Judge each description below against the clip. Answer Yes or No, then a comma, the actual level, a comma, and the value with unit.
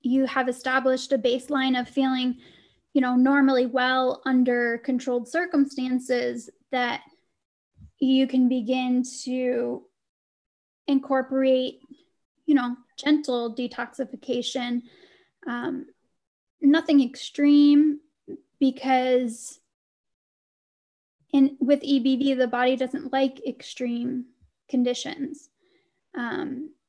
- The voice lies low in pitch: No, very high, 265 Hz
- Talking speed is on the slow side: Yes, slow, 85 wpm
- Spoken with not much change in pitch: Yes, narrow, 2.1 semitones